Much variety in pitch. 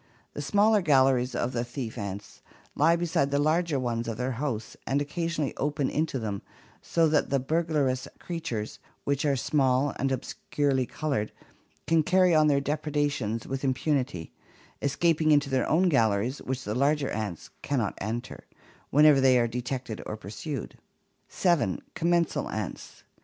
No: average, 4.0 semitones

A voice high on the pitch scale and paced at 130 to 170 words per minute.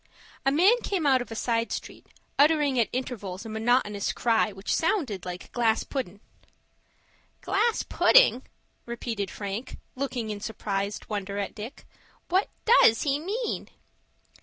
Yes: high, 235 Hz; slow, 135 wpm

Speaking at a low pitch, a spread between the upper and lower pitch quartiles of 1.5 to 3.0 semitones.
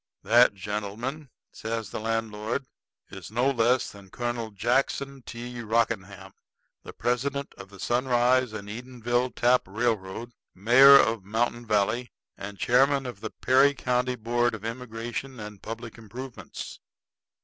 Yes: low, 120 Hz; average, 2.7 semitones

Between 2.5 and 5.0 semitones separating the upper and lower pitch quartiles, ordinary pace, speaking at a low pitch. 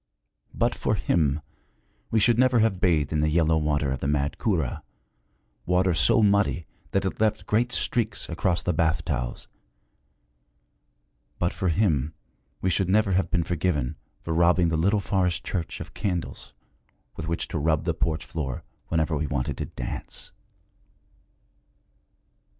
Yes: average, 4.0 semitones; average, 150 wpm; very low, 85 Hz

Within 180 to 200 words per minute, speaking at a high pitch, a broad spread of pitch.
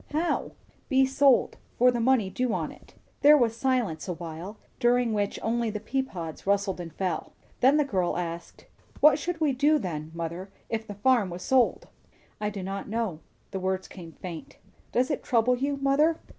Yes: average, 185 wpm; high, 225 Hz; wide, 6.1 semitones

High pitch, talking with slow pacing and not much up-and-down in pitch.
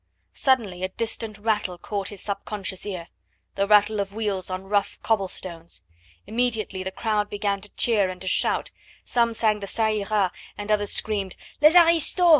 No: high, 205 Hz; average, 170 wpm; narrow, 2.3 semitones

